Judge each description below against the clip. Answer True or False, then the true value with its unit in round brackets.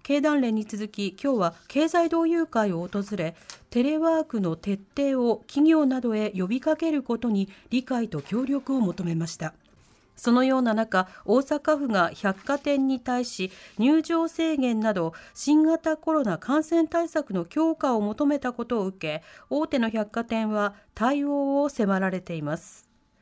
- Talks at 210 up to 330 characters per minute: True (285 characters per minute)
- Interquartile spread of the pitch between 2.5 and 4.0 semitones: False (6.3 semitones)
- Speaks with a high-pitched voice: True (240 Hz)